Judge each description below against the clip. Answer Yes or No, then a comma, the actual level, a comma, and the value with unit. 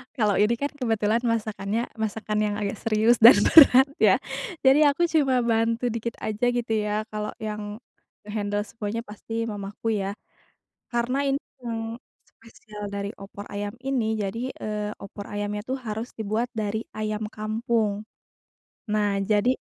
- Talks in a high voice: Yes, high, 220 Hz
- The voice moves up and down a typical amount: No, narrow, 2.1 semitones